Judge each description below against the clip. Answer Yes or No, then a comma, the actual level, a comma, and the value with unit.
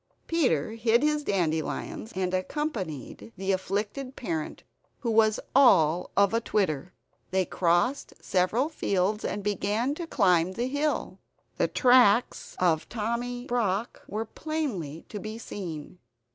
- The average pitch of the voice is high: Yes, high, 210 Hz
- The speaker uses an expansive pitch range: No, average, 5.0 semitones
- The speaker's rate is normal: No, slow, 125 wpm